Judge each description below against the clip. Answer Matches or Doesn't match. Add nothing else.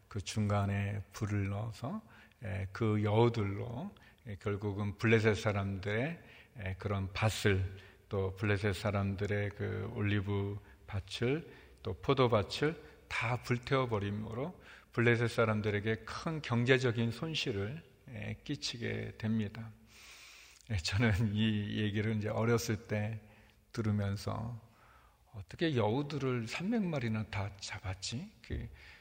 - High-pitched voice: Doesn't match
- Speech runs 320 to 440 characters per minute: Doesn't match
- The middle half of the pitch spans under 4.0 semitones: Matches